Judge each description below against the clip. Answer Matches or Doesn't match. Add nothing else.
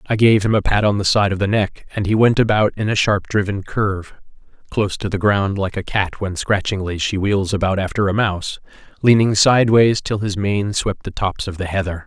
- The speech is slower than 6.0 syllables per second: Matches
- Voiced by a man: Matches